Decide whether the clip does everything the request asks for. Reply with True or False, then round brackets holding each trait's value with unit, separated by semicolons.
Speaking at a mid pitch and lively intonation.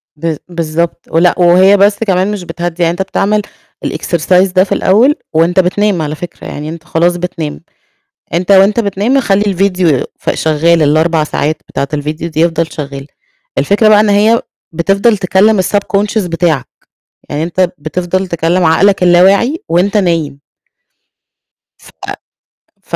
False (175 Hz; 3.3 semitones)